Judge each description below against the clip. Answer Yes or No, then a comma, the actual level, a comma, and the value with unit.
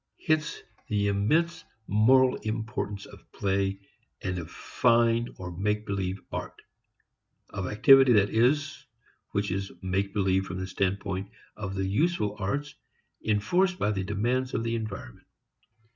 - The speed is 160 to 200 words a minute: No, slow, 135 wpm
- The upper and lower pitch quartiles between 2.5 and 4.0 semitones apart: Yes, average, 3.7 semitones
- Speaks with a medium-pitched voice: No, low, 105 Hz